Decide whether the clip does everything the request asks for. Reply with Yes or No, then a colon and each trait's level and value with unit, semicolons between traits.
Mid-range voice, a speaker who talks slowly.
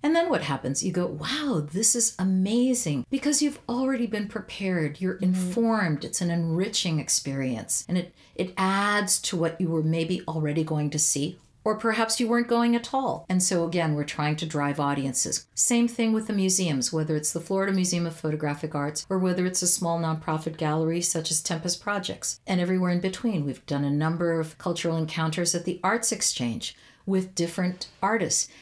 No: medium, 175 Hz; average, 190 wpm